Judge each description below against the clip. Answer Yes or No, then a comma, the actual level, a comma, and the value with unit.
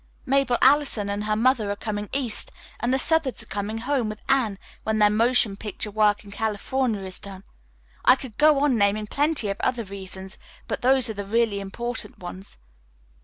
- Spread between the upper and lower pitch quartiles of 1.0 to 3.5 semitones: No, average, 4.0 semitones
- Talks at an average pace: Yes, average, 185 wpm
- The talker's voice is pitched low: No, high, 220 Hz